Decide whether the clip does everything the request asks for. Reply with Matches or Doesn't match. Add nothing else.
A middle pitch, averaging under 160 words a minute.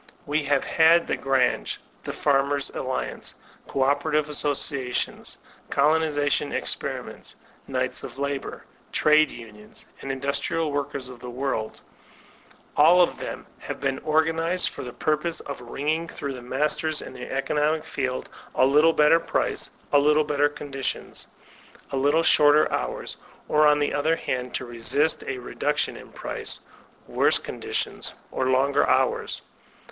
Matches